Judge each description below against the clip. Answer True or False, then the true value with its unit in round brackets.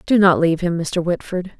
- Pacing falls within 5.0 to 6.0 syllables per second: True (5.4 syllables/s)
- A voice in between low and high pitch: True (175 Hz)